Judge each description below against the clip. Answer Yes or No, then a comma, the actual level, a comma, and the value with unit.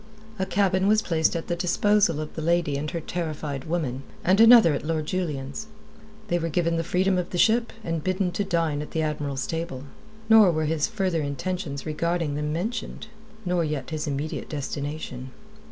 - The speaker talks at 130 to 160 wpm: No, average, 185 wpm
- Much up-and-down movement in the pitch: No, average, 3.6 semitones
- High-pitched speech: No, medium, 165 Hz